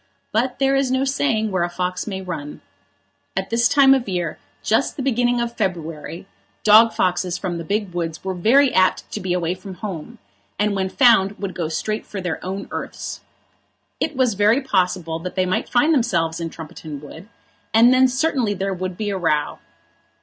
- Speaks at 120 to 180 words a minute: No, average, 195 wpm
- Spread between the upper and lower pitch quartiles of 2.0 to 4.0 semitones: No, average, 5.0 semitones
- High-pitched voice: Yes, high, 195 Hz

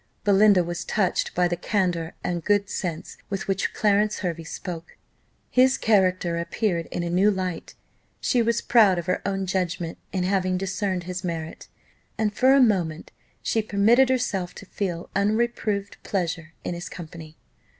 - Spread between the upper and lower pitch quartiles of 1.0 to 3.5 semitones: Yes, average, 3.2 semitones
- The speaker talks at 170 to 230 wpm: No, average, 160 wpm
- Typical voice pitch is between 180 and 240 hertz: Yes, high, 190 Hz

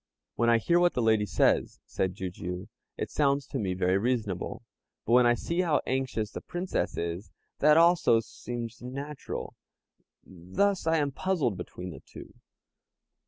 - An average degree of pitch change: No, wide, 7.3 semitones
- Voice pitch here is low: Yes, low, 120 Hz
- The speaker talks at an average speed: Yes, average, 160 wpm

